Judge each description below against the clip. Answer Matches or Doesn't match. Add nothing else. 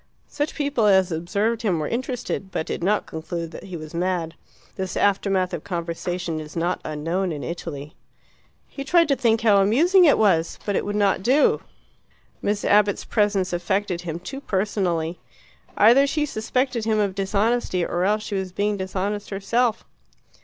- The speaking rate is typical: Matches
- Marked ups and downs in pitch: Doesn't match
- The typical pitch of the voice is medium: Doesn't match